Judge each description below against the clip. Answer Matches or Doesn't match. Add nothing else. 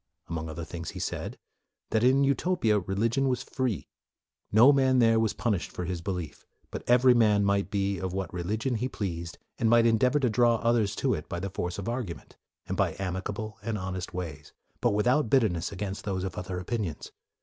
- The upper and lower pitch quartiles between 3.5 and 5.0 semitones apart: Matches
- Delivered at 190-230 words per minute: Matches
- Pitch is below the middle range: Matches